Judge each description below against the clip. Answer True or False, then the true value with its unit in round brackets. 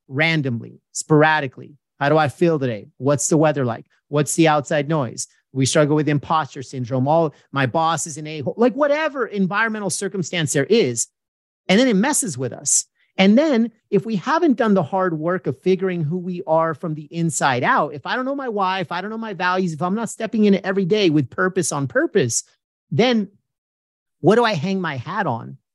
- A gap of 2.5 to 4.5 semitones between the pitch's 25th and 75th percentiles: False (5.1 semitones)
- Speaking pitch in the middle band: True (165 Hz)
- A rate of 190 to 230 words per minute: True (205 wpm)